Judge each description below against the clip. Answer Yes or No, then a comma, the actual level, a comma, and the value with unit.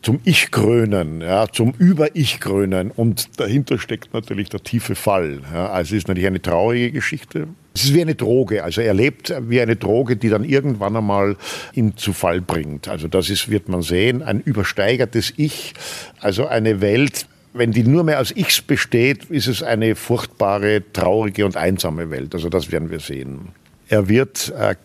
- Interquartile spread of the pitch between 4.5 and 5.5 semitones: Yes, average, 4.8 semitones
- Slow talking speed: No, average, 185 wpm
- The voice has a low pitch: Yes, low, 110 Hz